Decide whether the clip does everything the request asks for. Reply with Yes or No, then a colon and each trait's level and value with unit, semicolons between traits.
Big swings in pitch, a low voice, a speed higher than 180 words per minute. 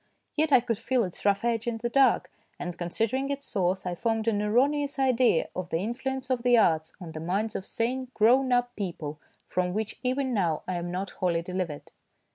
No: wide, 5.8 semitones; high, 220 Hz; fast, 205 wpm